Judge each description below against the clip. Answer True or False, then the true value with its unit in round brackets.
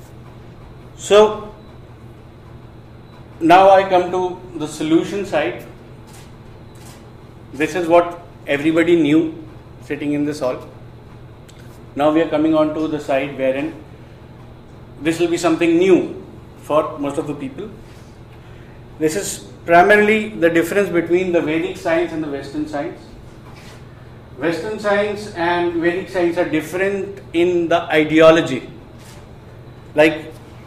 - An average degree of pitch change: False (6.3 semitones)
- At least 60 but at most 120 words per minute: True (115 wpm)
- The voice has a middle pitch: True (150 Hz)